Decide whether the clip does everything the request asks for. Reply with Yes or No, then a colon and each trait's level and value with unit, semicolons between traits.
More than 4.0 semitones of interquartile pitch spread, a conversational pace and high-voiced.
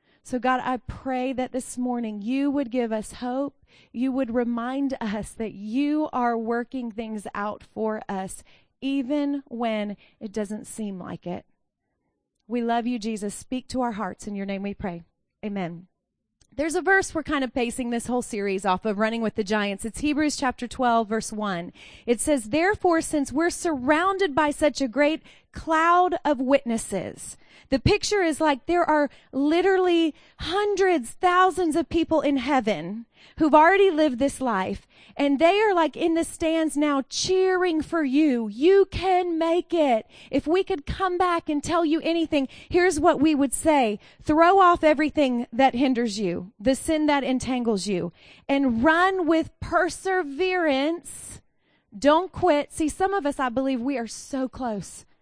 Yes: wide, 5.6 semitones; average, 175 wpm; very high, 275 Hz